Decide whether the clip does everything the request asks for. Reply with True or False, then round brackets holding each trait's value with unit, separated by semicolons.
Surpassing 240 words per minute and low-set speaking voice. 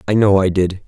True (275 wpm; 95 Hz)